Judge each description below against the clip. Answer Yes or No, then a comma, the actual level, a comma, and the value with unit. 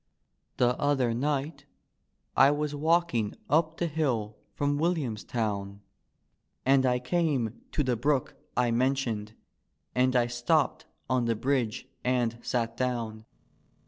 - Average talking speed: No, slow, 125 wpm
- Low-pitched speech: Yes, low, 125 Hz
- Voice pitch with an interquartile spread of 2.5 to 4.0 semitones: Yes, average, 3.7 semitones